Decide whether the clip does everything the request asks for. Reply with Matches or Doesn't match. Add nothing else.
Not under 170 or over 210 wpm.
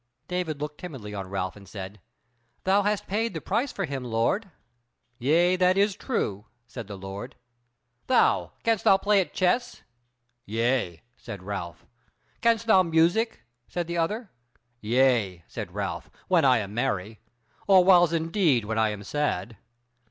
Doesn't match